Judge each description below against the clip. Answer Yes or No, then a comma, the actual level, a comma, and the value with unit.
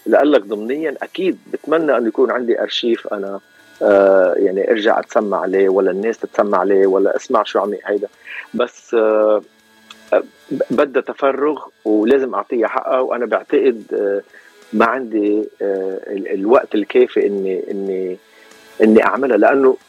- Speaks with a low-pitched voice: Yes, low, 110 Hz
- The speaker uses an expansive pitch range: Yes, wide, 7.5 semitones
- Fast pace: No, average, 120 wpm